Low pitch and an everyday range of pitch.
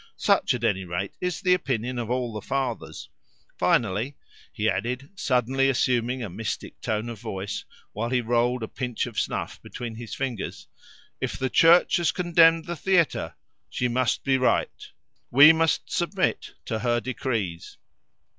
Yes: low, 125 Hz; average, 3.4 semitones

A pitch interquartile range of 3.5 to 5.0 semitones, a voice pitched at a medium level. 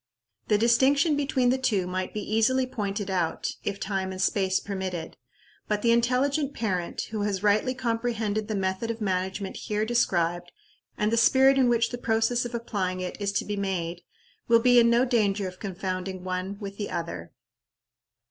No: average, 4.0 semitones; high, 210 Hz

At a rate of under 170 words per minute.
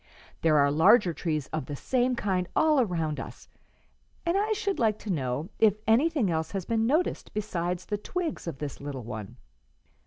No: average, 180 wpm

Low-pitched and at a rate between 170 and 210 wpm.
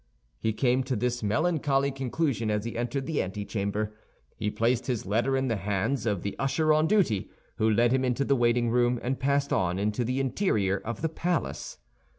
Yes: low, 120 Hz; average, 190 wpm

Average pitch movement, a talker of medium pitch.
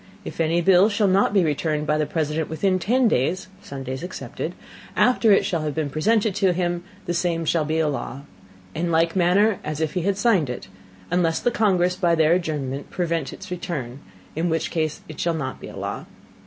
Yes: average, 3.2 semitones; medium, 170 Hz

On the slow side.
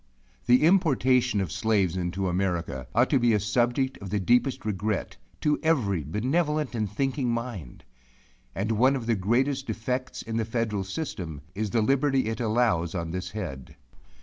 No: average, 165 wpm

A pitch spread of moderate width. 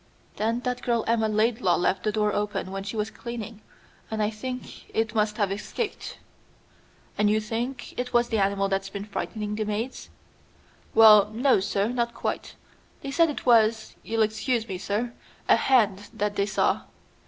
No: narrow, 2.3 semitones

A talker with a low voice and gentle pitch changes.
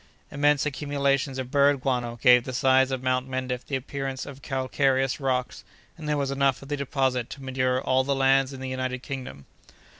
Yes: low, 130 Hz; narrow, 1.3 semitones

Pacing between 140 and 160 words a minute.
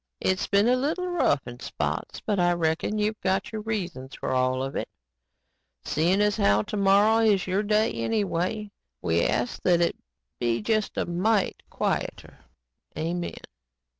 Yes: average, 155 wpm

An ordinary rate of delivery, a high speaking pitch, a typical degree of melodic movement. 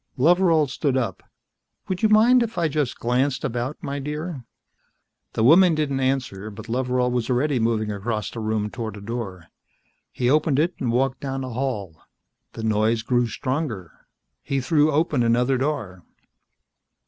No: average, 160 wpm; low, 130 Hz; average, 4.7 semitones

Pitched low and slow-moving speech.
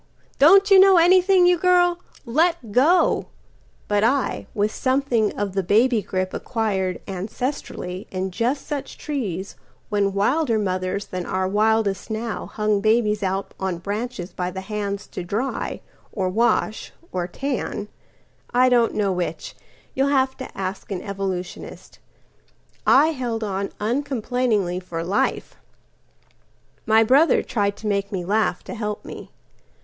No: high, 215 Hz; slow, 125 wpm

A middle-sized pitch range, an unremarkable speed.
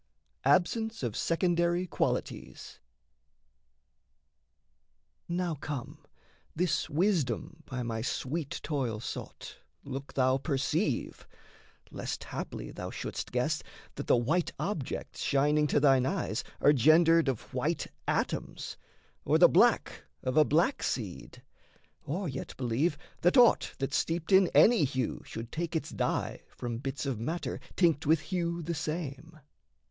No: average, 4.7 semitones; slow, 130 wpm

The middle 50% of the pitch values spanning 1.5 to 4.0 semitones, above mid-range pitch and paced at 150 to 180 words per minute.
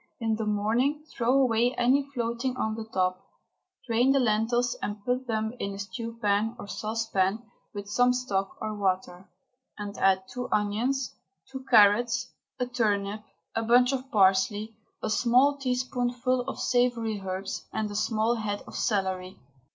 Yes: average, 3.3 semitones; high, 225 Hz; average, 155 wpm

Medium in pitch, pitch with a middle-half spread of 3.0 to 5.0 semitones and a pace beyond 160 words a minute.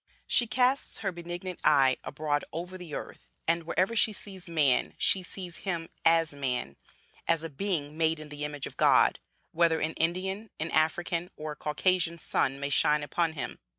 Yes: medium, 165 Hz; average, 3.4 semitones; average, 180 wpm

